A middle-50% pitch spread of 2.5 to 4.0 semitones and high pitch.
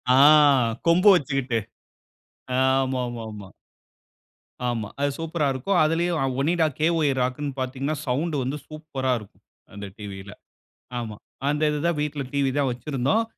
No: average, 3.7 semitones; low, 135 Hz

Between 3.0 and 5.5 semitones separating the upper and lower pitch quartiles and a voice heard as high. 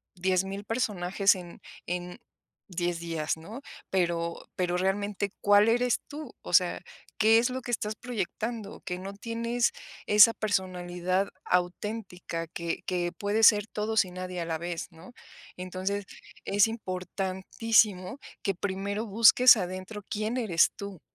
Yes: average, 3.3 semitones; high, 195 Hz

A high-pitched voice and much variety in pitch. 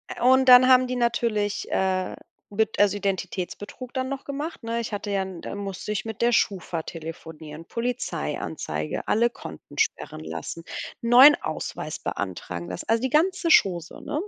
Yes: high, 205 Hz; wide, 6.8 semitones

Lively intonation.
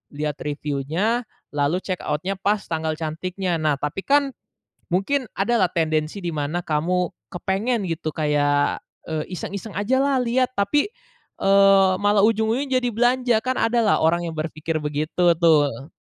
Yes: wide, 6.2 semitones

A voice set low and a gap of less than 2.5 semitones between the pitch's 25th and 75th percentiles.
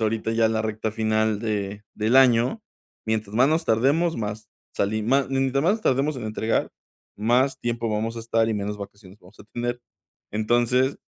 No: low, 115 Hz; average, 2.8 semitones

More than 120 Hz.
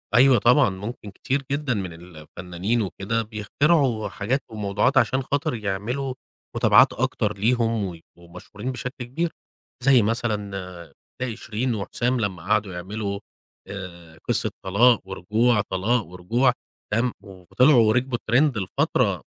No: low, 110 Hz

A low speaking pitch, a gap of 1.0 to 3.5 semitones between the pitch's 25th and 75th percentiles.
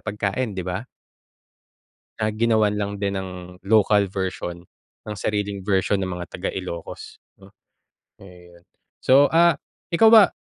Yes: low, 100 Hz; average, 2.7 semitones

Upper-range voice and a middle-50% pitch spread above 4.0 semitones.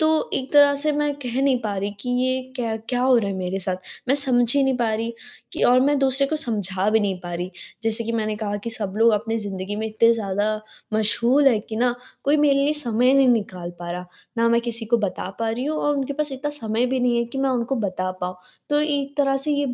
Yes: high, 235 Hz; average, 4.4 semitones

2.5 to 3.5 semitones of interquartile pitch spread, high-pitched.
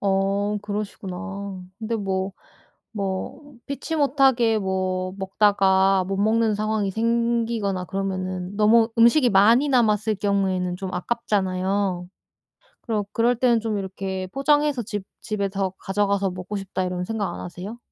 Yes: average, 3.0 semitones; high, 200 Hz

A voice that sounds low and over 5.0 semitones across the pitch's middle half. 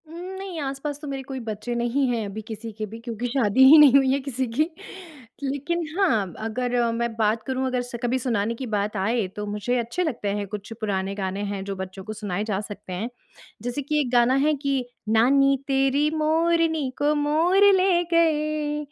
No: very high, 250 Hz; wide, 5.4 semitones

